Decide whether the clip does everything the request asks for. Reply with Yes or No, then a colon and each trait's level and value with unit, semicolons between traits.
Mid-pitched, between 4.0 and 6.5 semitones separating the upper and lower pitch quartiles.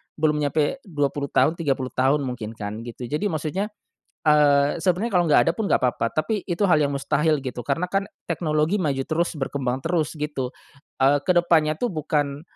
No: medium, 150 Hz; average, 3.3 semitones